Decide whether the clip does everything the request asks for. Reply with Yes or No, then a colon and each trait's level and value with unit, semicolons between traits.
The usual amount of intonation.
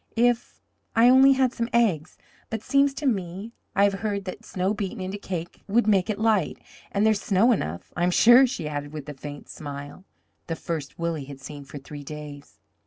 No: wide, 6.8 semitones